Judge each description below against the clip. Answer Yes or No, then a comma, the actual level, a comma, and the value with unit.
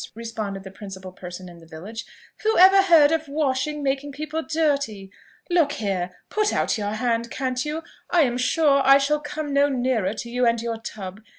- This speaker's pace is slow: No, average, 185 wpm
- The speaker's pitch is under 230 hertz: No, very high, 255 Hz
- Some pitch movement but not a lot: No, wide, 6.0 semitones